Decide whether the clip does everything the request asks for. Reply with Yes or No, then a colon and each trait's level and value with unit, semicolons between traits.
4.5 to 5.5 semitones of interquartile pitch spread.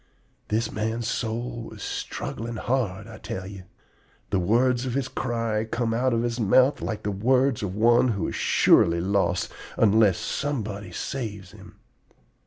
No: average, 2.9 semitones